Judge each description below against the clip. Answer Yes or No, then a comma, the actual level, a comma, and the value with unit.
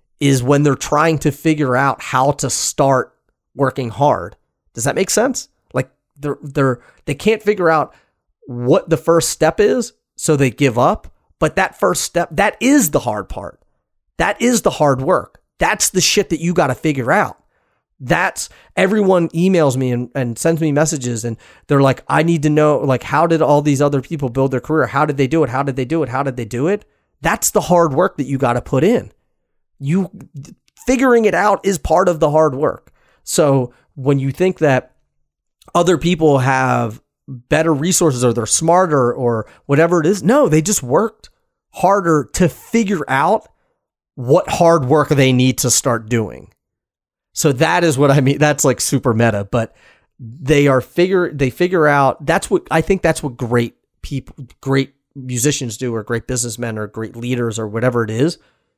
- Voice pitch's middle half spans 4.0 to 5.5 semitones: Yes, average, 4.5 semitones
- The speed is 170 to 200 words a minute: Yes, average, 190 wpm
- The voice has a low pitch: No, medium, 145 Hz